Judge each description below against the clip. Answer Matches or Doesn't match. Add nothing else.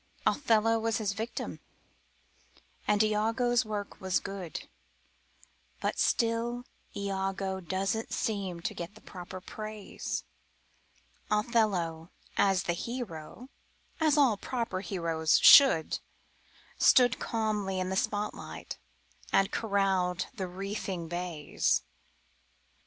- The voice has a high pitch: Matches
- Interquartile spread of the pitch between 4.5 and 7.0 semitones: Doesn't match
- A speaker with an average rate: Doesn't match